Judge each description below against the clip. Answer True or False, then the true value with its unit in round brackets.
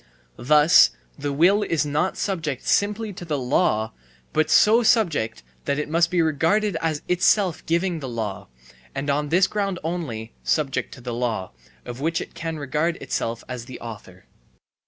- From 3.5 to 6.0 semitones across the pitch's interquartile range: True (5.6 semitones)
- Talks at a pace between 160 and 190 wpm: True (165 wpm)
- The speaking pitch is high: False (155 Hz)